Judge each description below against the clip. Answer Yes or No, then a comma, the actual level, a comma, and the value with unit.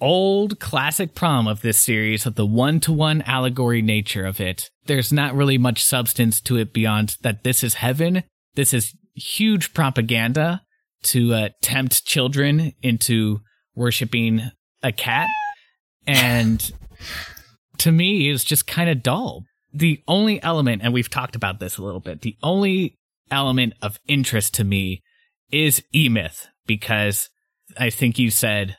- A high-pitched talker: No, low, 125 Hz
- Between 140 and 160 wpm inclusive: Yes, average, 150 wpm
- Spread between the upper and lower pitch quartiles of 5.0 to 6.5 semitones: Yes, wide, 5.6 semitones